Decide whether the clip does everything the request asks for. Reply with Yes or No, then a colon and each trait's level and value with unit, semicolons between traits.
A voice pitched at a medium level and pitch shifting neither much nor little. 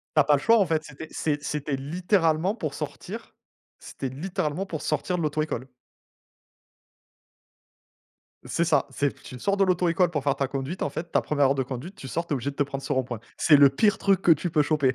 Yes: medium, 150 Hz; average, 4.0 semitones